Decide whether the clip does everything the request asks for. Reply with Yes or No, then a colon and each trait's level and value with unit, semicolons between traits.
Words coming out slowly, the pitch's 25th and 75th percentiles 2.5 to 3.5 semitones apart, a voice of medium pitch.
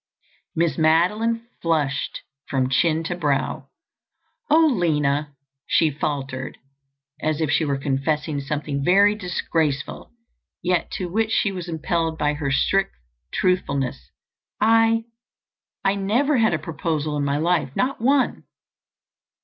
No: slow, 115 wpm; average, 5.3 semitones; medium, 165 Hz